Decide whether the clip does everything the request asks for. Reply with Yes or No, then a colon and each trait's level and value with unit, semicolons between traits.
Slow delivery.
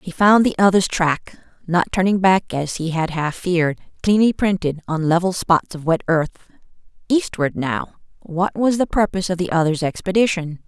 No: average, 170 wpm